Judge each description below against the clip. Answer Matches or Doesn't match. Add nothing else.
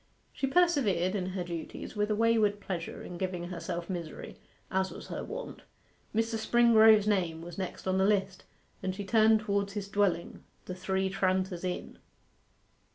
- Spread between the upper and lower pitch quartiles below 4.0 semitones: Matches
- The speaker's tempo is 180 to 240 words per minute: Doesn't match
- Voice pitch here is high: Matches